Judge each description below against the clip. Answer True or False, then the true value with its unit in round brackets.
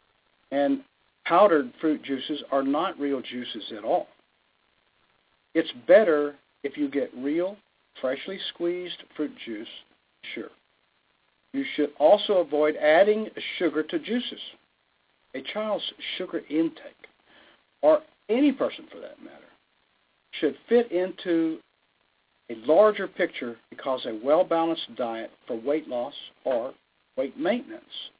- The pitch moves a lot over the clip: True (6.0 semitones)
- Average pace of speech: False (115 wpm)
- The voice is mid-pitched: True (160 Hz)